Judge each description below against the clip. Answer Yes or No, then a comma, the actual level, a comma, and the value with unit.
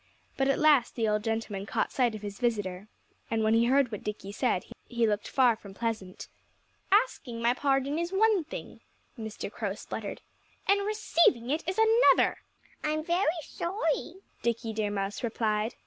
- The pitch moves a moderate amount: No, wide, 6.4 semitones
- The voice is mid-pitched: No, high, 235 Hz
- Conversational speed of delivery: Yes, average, 165 wpm